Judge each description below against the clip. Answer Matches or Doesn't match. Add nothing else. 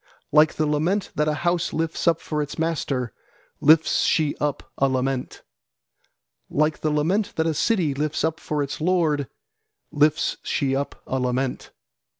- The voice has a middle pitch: Matches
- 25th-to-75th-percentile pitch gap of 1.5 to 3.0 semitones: Matches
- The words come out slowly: Doesn't match